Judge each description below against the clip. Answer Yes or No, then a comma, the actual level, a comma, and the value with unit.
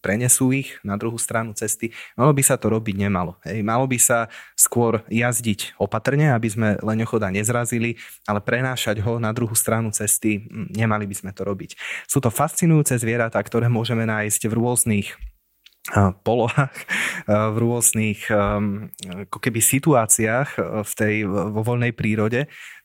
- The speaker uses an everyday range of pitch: No, narrow, 2.2 semitones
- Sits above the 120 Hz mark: No, low, 115 Hz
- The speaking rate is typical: Yes, average, 140 wpm